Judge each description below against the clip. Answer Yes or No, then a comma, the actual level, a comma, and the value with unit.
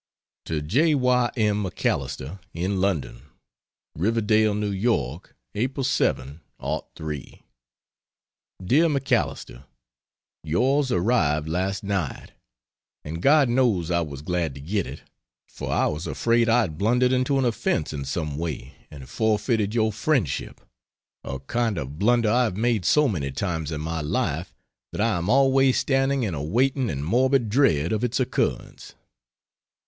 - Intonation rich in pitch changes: Yes, wide, 7.6 semitones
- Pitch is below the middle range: Yes, low, 105 Hz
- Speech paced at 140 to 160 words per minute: Yes, average, 145 wpm